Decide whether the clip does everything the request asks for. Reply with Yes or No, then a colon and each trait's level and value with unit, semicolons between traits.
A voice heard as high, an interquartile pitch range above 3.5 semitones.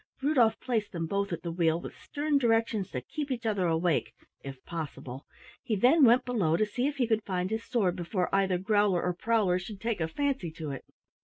Yes: high, 200 Hz; average, 5.2 semitones